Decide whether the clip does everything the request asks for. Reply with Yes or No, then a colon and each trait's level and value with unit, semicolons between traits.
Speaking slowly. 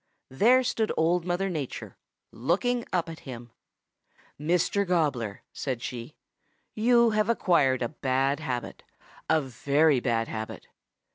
Yes: slow, 125 wpm